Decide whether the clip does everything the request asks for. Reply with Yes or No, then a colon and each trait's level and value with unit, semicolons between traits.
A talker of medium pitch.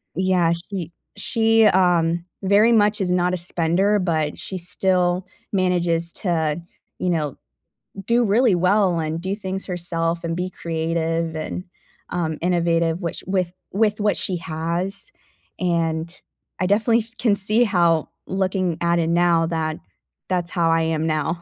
Yes: medium, 175 Hz